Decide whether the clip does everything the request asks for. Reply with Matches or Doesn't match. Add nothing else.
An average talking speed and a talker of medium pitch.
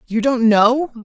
Doesn't match